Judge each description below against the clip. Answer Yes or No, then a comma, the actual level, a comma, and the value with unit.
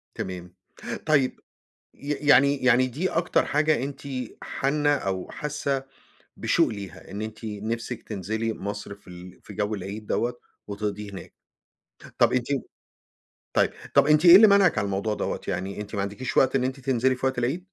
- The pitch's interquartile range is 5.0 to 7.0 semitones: Yes, wide, 5.5 semitones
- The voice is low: Yes, low, 120 Hz